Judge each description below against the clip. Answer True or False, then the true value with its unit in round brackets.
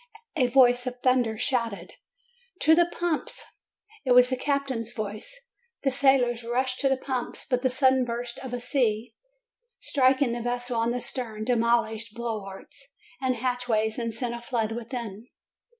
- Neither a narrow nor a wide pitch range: False (2.1 semitones)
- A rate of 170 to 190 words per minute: False (160 wpm)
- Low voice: False (245 Hz)